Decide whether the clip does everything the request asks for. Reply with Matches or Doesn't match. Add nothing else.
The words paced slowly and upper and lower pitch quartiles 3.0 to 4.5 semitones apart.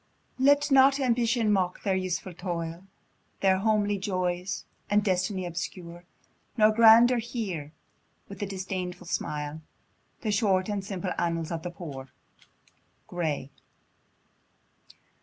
Matches